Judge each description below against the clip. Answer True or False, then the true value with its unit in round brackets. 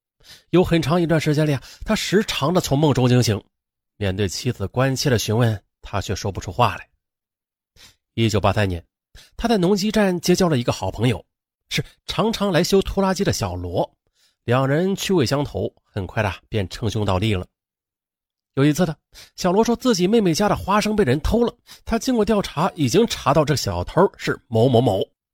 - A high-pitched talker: False (125 Hz)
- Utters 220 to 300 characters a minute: True (270 characters per minute)